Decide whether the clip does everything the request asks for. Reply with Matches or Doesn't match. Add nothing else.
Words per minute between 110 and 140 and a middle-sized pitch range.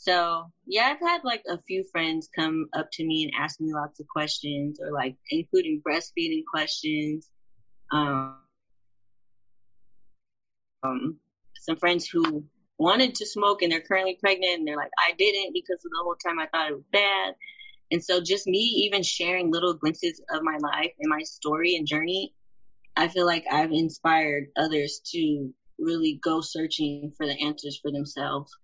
Doesn't match